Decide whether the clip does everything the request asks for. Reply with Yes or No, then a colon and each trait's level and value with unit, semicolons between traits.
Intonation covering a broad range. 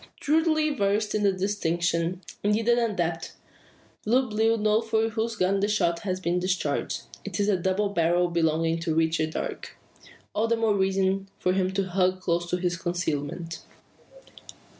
No: average, 3.5 semitones